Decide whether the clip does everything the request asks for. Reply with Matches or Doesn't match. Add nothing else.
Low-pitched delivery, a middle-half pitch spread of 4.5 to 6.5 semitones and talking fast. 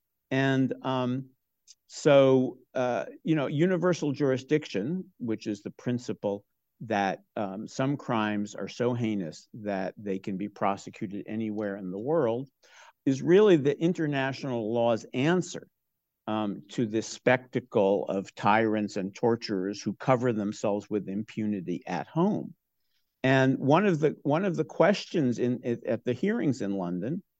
Doesn't match